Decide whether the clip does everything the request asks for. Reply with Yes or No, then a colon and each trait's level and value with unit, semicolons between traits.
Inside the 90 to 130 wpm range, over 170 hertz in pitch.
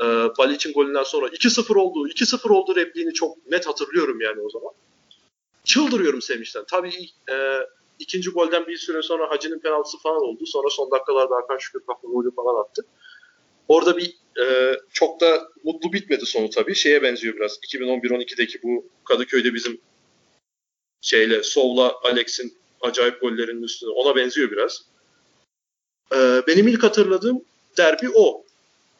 No: fast, 140 wpm; medium, 185 Hz